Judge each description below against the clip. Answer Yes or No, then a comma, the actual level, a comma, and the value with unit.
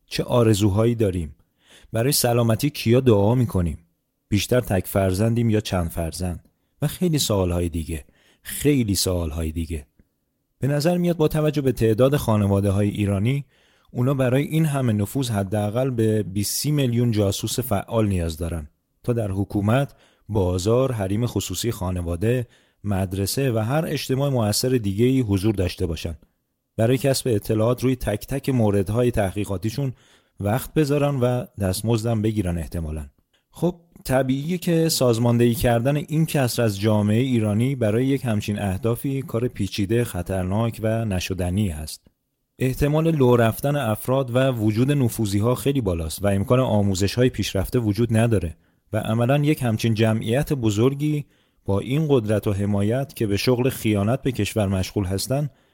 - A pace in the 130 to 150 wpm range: Yes, average, 140 wpm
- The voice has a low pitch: Yes, low, 115 Hz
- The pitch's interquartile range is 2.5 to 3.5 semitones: No, average, 4.7 semitones